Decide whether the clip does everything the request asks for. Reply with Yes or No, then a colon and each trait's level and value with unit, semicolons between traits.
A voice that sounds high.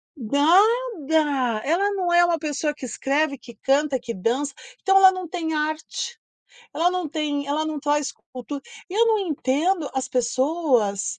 Yes: very high, 300 Hz